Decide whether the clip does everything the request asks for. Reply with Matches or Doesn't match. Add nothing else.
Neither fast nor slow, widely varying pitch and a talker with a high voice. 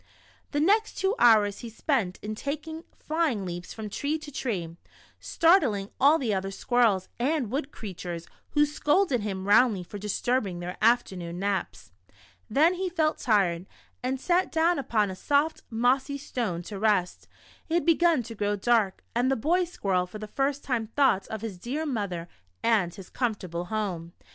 Matches